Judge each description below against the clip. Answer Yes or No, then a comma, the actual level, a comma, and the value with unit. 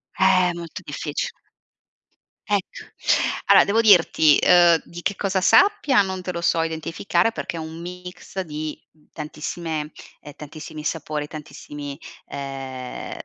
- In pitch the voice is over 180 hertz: No, medium, 165 Hz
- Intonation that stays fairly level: No, average, 3.6 semitones